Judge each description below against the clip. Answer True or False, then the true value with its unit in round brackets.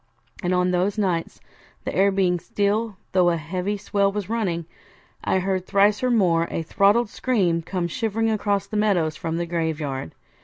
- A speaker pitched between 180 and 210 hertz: True (190 Hz)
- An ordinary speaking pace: True (170 wpm)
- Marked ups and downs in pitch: False (3.3 semitones)